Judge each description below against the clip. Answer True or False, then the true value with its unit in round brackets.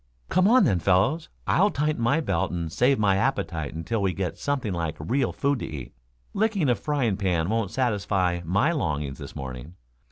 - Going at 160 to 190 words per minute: True (185 wpm)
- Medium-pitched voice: False (100 Hz)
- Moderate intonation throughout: False (8.4 semitones)